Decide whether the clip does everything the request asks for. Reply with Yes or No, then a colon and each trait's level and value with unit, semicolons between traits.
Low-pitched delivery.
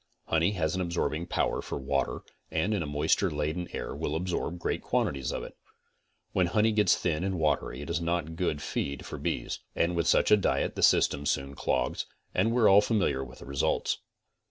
Yes: very low, 85 Hz